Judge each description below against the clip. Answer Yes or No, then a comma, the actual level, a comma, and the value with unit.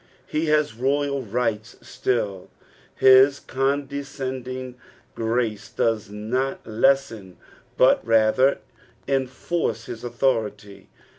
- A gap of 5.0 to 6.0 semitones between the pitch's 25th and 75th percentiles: No, average, 3.5 semitones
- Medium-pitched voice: No, low, 125 Hz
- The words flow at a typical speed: No, slow, 90 wpm